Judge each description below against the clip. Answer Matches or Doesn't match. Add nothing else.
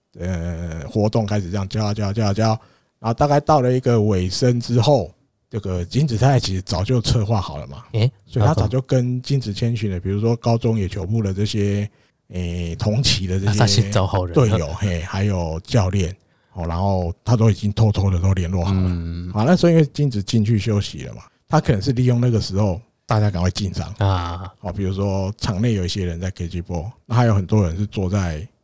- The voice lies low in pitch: Matches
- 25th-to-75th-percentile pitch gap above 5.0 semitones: Doesn't match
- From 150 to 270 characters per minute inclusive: Doesn't match